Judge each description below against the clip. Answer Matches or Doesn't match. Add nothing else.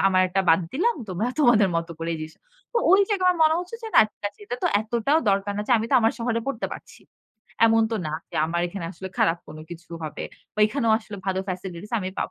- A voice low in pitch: Doesn't match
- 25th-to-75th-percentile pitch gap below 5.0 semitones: Doesn't match